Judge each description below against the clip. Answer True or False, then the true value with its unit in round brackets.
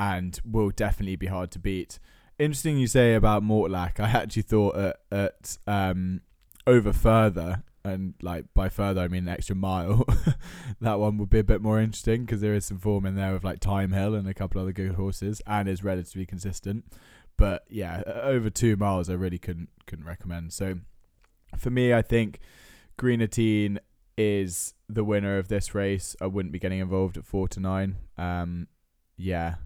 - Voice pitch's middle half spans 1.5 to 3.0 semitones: True (2.5 semitones)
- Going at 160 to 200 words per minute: True (185 wpm)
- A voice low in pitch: True (100 Hz)